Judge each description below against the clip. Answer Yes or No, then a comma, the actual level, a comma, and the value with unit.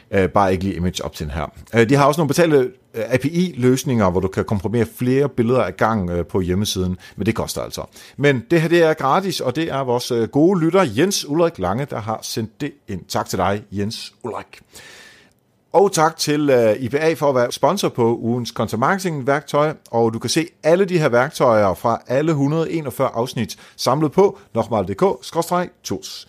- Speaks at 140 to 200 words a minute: Yes, average, 185 wpm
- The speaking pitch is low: Yes, low, 125 Hz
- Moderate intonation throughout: No, wide, 6.7 semitones